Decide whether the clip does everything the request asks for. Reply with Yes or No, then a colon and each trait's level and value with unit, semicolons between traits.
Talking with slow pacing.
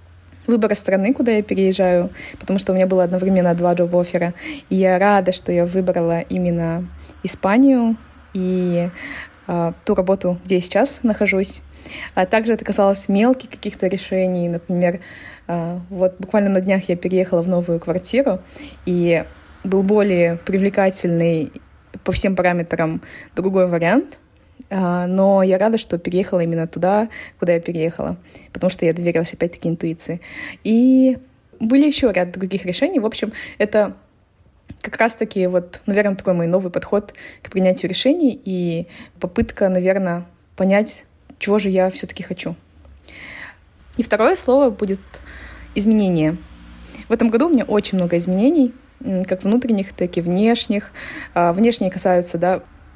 No: average, 140 wpm